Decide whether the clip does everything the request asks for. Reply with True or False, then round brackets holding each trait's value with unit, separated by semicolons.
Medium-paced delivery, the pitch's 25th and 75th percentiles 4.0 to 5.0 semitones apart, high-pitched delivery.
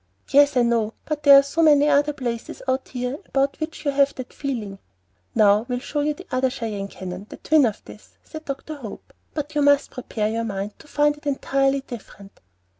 False (210 wpm; 4.3 semitones; 270 Hz)